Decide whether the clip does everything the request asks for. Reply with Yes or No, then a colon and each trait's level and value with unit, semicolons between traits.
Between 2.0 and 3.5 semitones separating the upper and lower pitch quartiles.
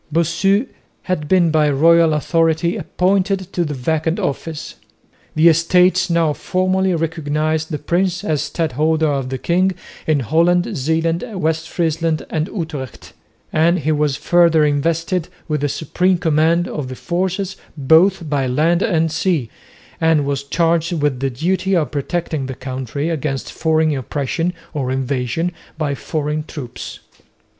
Yes: average, 2.7 semitones